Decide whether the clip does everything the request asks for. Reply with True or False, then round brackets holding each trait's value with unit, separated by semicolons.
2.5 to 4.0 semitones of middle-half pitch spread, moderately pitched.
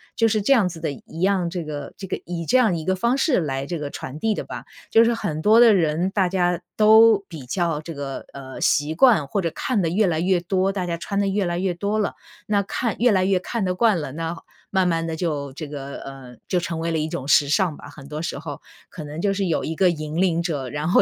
False (4.4 semitones; 175 Hz)